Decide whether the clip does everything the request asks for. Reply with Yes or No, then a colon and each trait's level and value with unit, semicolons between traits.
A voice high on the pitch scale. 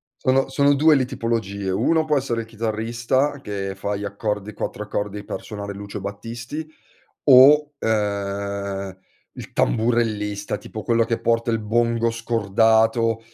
No: low, 115 Hz